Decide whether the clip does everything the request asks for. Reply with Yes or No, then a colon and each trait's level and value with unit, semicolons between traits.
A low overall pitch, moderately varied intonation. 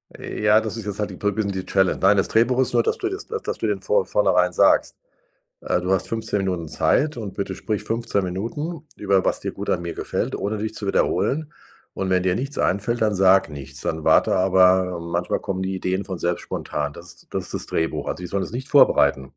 Yes: very low, 95 Hz; average, 3.3 semitones